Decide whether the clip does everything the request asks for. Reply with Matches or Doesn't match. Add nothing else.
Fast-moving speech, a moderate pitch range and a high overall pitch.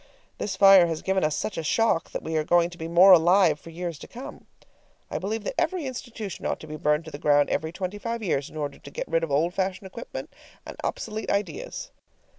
Doesn't match